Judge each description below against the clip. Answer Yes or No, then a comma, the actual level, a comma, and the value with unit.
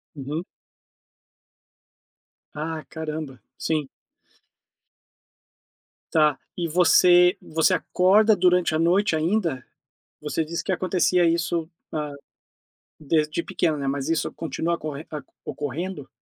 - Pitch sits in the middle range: Yes, medium, 160 Hz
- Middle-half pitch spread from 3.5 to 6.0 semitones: No, average, 2.8 semitones